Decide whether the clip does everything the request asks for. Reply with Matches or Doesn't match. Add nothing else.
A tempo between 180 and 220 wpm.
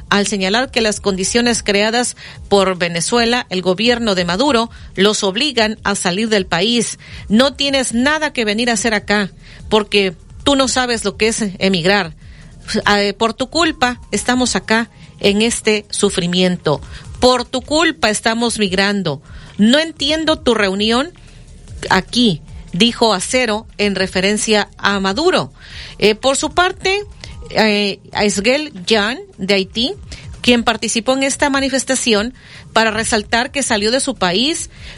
Doesn't match